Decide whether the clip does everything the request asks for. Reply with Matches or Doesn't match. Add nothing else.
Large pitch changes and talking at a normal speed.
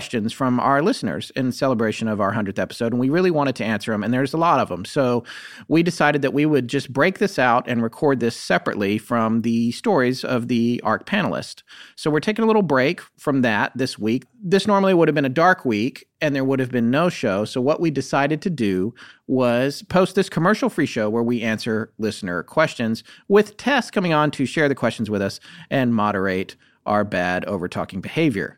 Doesn't match